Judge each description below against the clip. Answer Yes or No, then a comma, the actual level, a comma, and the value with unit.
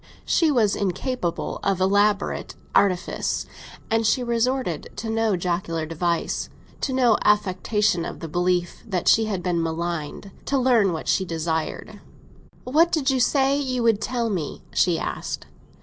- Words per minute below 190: Yes, average, 140 wpm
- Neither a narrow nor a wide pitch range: No, wide, 5.7 semitones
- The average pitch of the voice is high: Yes, high, 200 Hz